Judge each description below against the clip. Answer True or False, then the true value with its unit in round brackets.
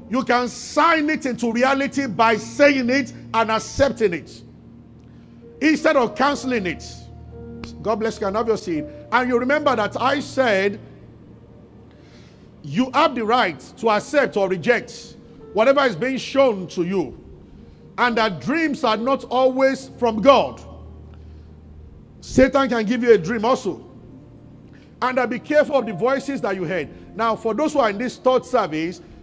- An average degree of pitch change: True (4.5 semitones)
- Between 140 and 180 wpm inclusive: True (160 wpm)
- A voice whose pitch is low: False (240 Hz)